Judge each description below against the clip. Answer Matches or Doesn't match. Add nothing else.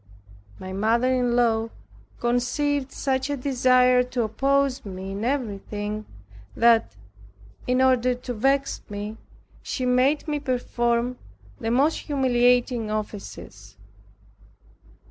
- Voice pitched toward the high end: Matches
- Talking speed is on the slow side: Matches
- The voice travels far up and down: Doesn't match